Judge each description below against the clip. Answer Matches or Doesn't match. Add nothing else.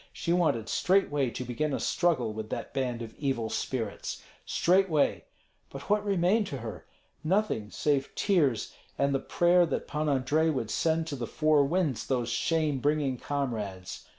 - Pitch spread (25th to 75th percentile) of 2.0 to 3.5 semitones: Doesn't match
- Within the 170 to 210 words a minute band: Doesn't match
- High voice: Doesn't match